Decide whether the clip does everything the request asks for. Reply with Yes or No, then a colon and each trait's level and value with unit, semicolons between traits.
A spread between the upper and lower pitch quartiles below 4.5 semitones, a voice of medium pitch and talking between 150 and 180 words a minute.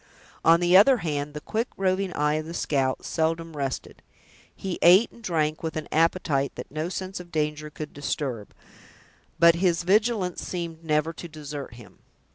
Yes: average, 3.2 semitones; medium, 165 Hz; average, 170 wpm